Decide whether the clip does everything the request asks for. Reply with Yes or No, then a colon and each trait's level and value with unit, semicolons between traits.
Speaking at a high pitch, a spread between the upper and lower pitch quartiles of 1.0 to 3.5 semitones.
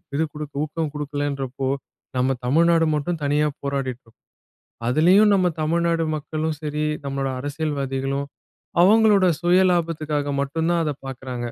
No: medium, 150 Hz; average, 3.2 semitones